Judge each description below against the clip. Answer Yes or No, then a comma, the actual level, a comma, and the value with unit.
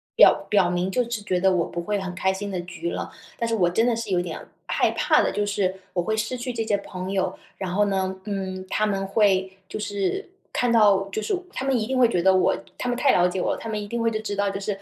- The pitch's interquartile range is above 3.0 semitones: No, average, 2.7 semitones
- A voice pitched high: Yes, high, 200 Hz